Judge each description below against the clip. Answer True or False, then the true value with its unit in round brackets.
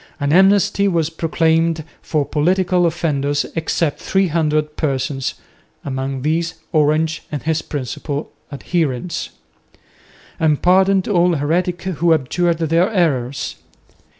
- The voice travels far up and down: False (3.2 semitones)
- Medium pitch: True (160 Hz)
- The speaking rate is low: True (115 wpm)